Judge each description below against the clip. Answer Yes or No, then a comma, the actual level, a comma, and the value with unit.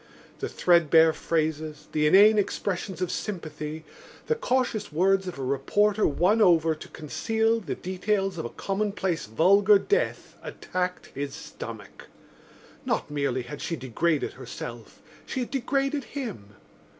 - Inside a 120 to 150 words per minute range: Yes, slow, 135 wpm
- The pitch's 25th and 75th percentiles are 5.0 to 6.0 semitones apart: Yes, wide, 5.4 semitones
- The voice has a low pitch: No, medium, 180 Hz